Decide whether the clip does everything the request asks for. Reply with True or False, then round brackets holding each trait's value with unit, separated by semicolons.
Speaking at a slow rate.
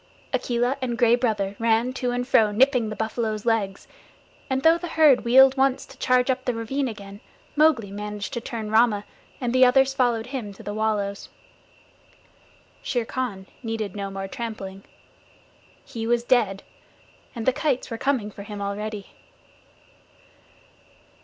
False (155 wpm)